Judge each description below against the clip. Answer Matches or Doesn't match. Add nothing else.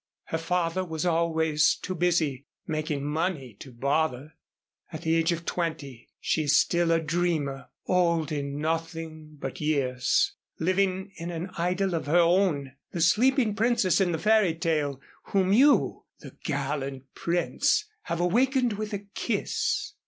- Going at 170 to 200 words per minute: Doesn't match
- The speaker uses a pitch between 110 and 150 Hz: Doesn't match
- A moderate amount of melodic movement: Matches